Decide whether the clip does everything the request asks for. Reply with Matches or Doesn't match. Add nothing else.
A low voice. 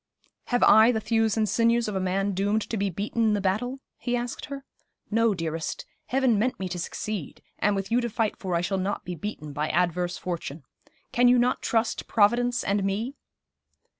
Doesn't match